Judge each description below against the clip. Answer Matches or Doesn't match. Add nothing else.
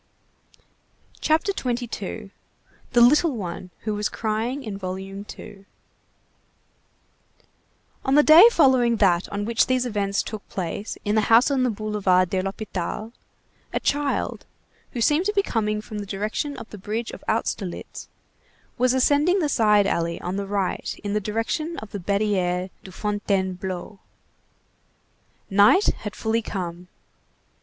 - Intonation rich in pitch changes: Doesn't match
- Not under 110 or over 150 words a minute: Matches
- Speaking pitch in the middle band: Doesn't match